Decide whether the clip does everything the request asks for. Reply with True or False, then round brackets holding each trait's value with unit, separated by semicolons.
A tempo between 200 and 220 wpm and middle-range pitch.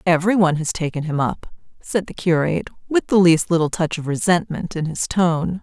True (205 wpm; 170 Hz)